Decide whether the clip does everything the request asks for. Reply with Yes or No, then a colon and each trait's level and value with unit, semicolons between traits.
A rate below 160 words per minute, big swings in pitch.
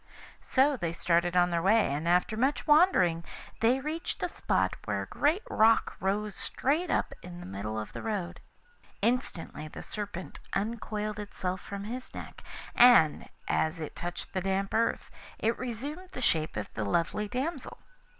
No: average, 165 wpm; wide, 6.4 semitones